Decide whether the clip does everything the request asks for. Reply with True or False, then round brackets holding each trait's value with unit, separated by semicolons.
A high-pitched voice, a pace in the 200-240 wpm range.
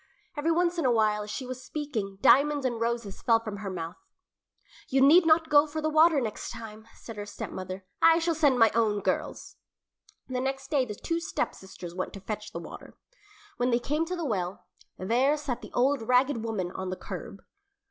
True (245 Hz; 205 wpm)